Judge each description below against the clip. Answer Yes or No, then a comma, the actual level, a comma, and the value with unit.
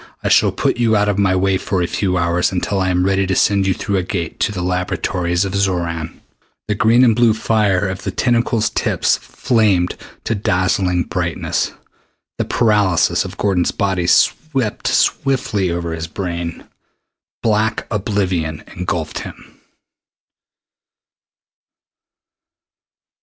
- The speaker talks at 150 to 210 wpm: No, average, 140 wpm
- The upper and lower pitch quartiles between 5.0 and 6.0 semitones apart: No, average, 3.0 semitones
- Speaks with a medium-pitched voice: No, very low, 95 Hz